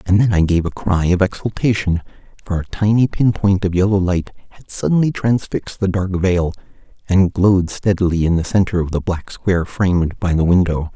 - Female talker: No, male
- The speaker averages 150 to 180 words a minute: No, average, 190 wpm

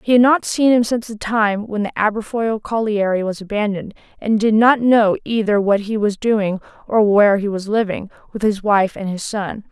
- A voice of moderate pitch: No, high, 210 Hz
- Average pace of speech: No, fast, 210 wpm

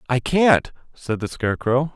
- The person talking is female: No, male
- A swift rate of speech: No, average, 155 wpm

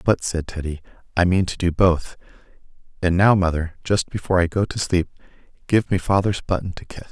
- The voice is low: Yes, very low, 90 Hz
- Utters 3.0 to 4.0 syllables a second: No, 5.7 syllables/s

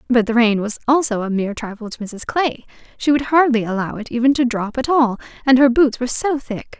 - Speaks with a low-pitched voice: No, high, 245 Hz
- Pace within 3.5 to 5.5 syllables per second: No, 5.7 syllables/s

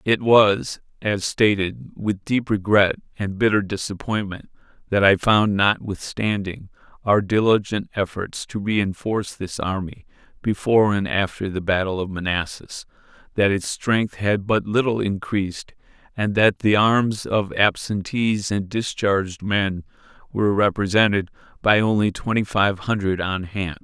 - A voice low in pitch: Yes, low, 100 Hz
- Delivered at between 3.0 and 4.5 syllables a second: Yes, 4.3 syllables/s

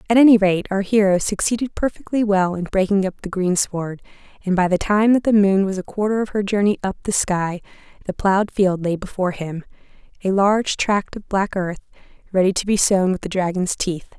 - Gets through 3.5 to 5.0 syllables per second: No, 5.6 syllables/s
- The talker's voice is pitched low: No, high, 195 Hz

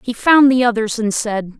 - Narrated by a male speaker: No, female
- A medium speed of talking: No, fast, 225 wpm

